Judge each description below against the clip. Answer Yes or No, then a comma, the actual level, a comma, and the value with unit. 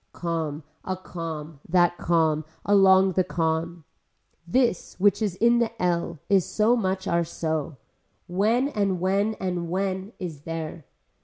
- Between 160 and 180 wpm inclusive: No, average, 140 wpm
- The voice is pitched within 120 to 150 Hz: No, medium, 180 Hz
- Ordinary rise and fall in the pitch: Yes, average, 3.2 semitones